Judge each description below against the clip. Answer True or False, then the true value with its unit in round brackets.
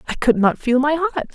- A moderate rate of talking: False (265 wpm)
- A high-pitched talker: True (280 Hz)